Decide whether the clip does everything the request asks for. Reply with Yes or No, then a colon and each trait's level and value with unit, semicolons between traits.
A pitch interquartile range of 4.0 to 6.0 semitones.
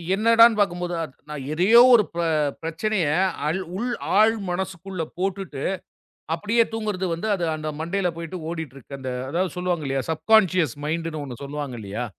Yes: average, 4.5 semitones